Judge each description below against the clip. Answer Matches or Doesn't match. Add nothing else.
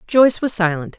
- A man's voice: Doesn't match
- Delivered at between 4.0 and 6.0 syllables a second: Matches